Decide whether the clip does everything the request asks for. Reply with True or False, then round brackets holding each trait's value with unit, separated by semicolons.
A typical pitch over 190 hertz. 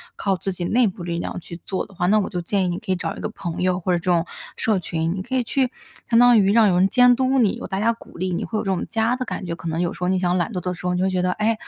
False (185 Hz)